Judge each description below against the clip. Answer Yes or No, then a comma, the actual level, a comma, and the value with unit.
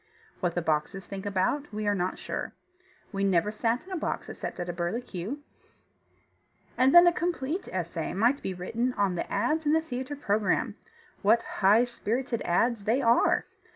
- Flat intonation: No, wide, 5.5 semitones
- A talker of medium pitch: No, high, 220 Hz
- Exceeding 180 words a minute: No, average, 175 wpm